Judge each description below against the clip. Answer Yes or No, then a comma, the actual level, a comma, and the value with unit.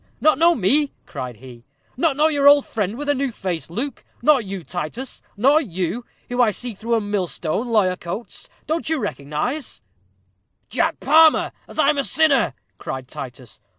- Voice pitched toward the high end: Yes, high, 235 Hz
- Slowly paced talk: No, average, 175 wpm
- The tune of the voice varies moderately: No, wide, 8.1 semitones